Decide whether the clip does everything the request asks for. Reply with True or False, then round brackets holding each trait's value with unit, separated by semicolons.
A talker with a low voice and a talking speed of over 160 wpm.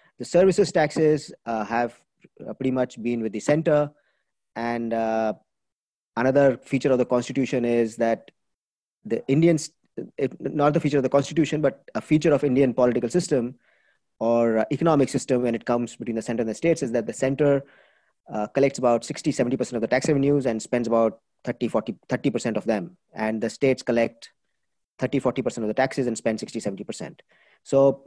True (130 Hz; 170 wpm)